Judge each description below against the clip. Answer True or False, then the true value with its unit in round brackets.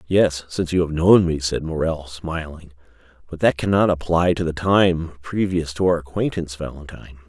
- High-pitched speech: False (80 Hz)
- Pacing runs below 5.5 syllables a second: True (5.2 syllables/s)